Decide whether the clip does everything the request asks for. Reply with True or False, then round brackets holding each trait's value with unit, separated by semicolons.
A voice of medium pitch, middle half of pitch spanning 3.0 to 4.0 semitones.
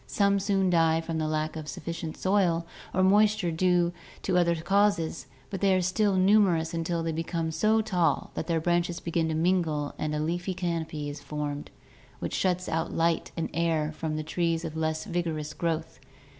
False (165 Hz; 2.4 semitones)